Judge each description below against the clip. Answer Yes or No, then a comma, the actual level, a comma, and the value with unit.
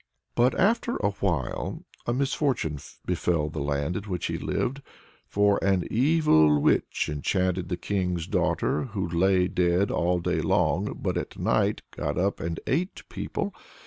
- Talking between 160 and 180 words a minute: No, average, 150 wpm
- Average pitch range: Yes, average, 4.0 semitones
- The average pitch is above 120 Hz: No, very low, 90 Hz